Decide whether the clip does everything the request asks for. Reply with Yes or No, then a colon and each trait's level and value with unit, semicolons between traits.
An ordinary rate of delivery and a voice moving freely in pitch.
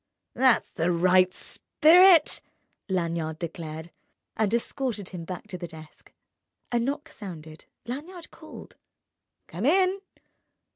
No: slow, 105 wpm; wide, 8.6 semitones